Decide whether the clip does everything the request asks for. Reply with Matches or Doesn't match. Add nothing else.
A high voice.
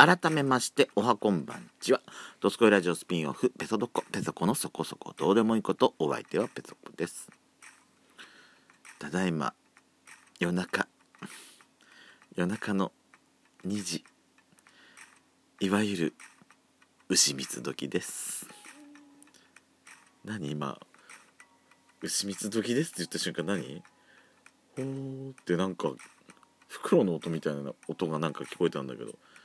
Doesn't match